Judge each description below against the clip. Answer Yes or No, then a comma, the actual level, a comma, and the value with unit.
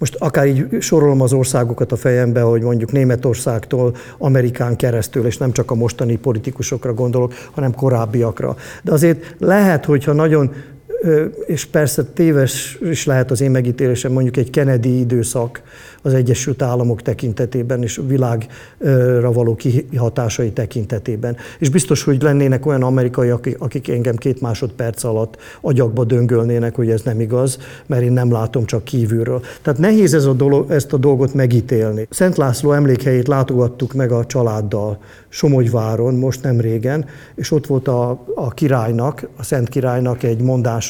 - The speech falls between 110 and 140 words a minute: No, average, 150 wpm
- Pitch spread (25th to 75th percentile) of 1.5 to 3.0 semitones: Yes, narrow, 2.6 semitones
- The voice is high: No, low, 125 Hz